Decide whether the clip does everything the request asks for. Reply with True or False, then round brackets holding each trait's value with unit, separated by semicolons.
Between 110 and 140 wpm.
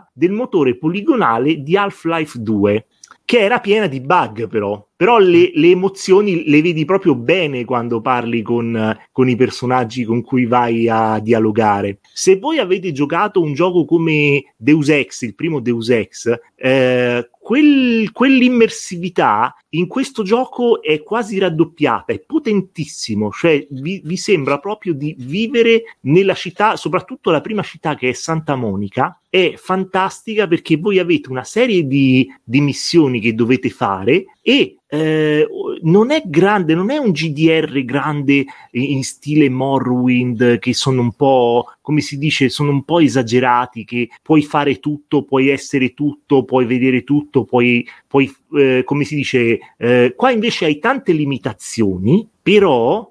False (150 wpm)